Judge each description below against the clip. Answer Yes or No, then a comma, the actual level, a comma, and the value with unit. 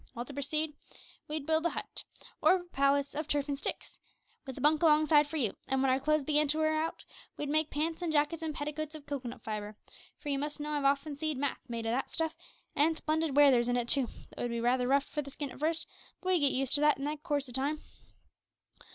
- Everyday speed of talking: No, fast, 250 wpm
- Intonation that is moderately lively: No, narrow, 2.3 semitones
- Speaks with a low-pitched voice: No, very high, 290 Hz